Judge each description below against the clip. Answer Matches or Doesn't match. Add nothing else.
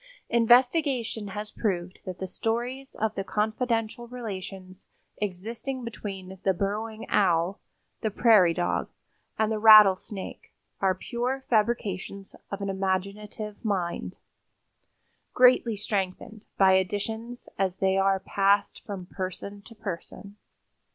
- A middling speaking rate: Doesn't match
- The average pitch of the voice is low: Doesn't match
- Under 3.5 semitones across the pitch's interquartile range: Matches